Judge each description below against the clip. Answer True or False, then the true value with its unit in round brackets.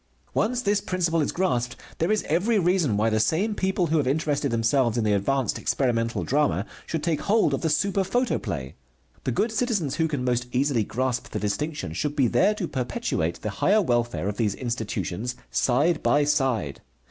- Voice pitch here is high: False (140 Hz)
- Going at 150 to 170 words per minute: False (185 wpm)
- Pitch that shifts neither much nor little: False (7.0 semitones)